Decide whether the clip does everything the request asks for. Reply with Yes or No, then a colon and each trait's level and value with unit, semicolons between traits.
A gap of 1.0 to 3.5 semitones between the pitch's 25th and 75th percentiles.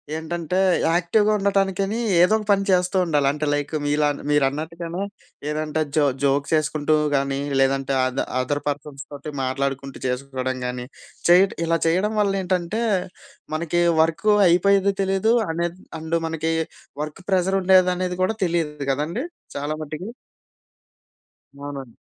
No: average, 4.3 semitones